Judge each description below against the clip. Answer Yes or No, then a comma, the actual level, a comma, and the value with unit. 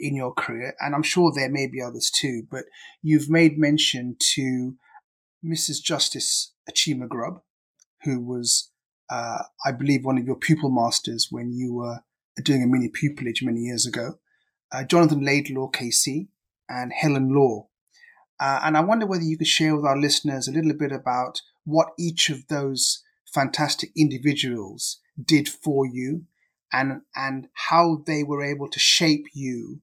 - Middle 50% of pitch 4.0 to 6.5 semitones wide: No, average, 3.3 semitones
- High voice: No, medium, 140 Hz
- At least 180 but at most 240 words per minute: No, average, 160 wpm